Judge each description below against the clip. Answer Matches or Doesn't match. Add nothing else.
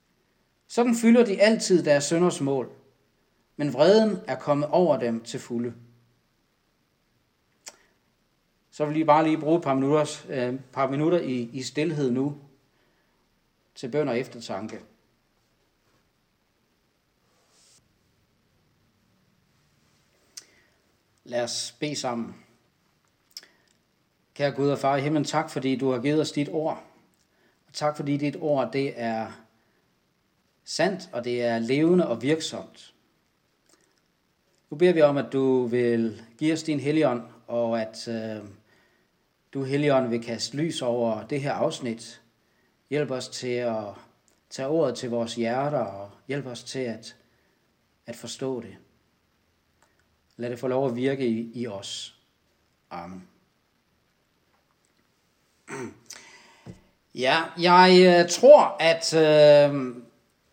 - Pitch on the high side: Doesn't match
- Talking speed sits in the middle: Doesn't match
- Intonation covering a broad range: Doesn't match